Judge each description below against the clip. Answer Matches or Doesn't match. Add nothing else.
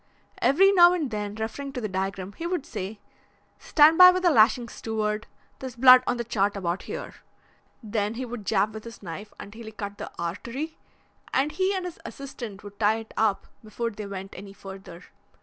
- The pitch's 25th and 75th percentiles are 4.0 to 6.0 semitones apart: Matches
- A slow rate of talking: Doesn't match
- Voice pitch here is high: Matches